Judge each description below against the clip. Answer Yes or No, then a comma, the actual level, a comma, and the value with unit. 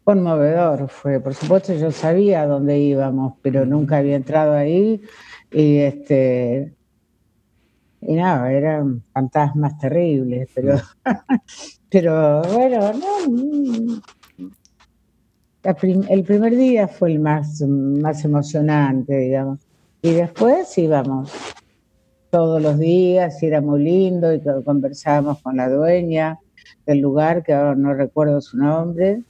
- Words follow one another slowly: Yes, slow, 120 wpm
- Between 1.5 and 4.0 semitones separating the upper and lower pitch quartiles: No, average, 4.6 semitones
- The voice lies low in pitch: No, medium, 150 Hz